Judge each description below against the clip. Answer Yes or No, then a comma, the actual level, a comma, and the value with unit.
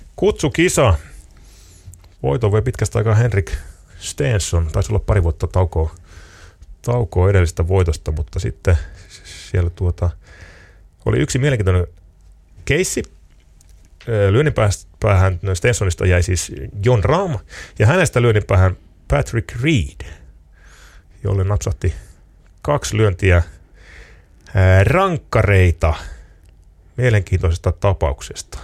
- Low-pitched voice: Yes, very low, 95 Hz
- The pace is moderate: No, slow, 85 wpm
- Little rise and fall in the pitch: No, average, 4.2 semitones